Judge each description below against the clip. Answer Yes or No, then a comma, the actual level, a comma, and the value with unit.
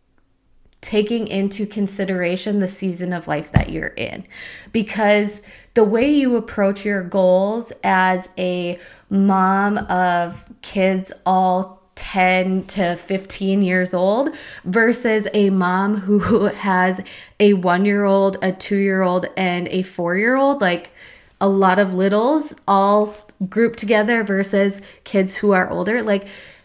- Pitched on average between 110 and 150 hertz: No, high, 195 Hz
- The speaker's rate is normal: No, slow, 120 wpm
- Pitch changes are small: Yes, narrow, 2.1 semitones